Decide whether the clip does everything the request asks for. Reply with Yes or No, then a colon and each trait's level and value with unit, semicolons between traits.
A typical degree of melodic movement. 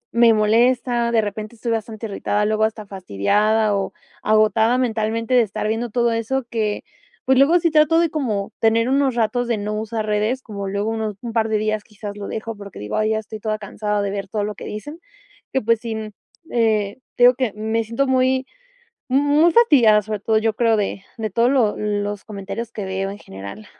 No: narrow, 2.2 semitones